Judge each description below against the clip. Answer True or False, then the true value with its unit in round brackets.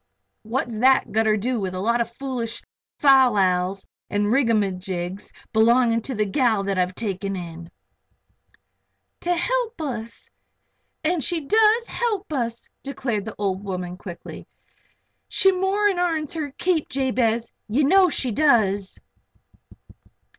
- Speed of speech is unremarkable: False (130 wpm)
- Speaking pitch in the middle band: False (235 Hz)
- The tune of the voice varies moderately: False (6.9 semitones)